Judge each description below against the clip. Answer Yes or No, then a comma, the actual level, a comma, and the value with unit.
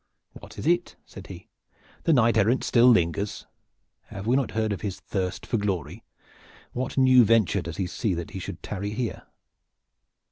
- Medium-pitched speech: No, low, 105 Hz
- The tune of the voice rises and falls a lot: No, average, 4.1 semitones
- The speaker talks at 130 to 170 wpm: Yes, average, 165 wpm